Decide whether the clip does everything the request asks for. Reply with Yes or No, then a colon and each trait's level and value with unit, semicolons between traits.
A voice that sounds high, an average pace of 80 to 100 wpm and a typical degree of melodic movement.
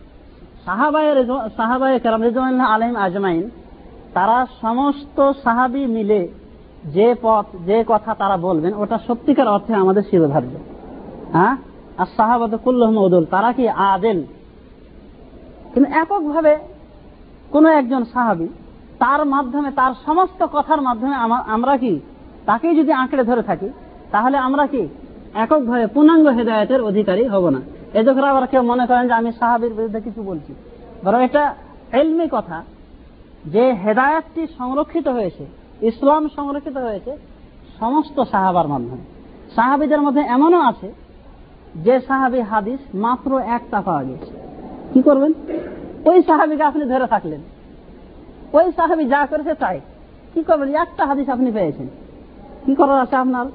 No: very high, 255 Hz; average, 115 wpm; average, 4.6 semitones